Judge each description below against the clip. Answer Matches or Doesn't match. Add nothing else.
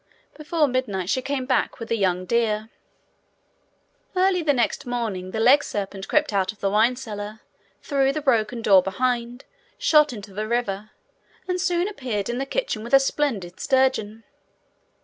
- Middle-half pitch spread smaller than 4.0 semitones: Doesn't match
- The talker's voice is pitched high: Matches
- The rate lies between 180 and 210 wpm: Doesn't match